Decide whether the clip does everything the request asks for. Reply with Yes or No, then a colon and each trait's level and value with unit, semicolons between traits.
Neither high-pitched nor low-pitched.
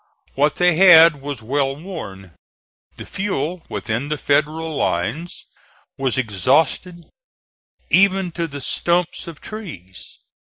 Yes: medium, 150 Hz